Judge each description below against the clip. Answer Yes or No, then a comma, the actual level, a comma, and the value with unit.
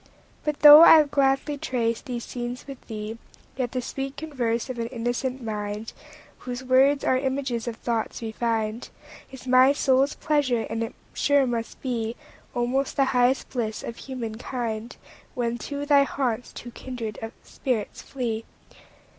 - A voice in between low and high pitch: No, very high, 250 Hz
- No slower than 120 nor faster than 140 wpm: Yes, slow, 135 wpm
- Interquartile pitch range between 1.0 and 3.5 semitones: Yes, average, 2.7 semitones